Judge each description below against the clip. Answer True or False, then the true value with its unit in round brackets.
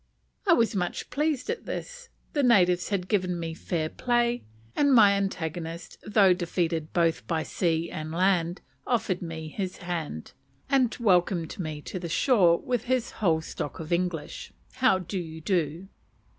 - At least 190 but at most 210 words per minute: False (155 wpm)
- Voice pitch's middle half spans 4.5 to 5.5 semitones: True (4.8 semitones)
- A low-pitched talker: False (180 Hz)